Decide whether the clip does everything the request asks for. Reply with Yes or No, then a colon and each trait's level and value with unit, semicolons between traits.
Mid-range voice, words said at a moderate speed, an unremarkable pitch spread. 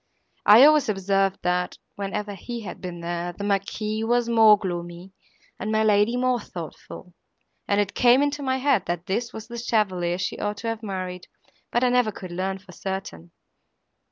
No: high, 205 Hz; average, 180 wpm; average, 4.1 semitones